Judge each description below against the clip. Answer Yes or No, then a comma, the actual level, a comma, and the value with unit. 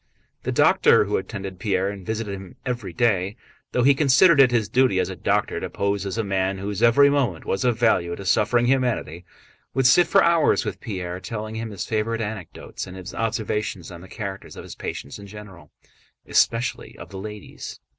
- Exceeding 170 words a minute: Yes, average, 200 wpm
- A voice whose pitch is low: Yes, low, 105 Hz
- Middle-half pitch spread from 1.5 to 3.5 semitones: No, average, 3.9 semitones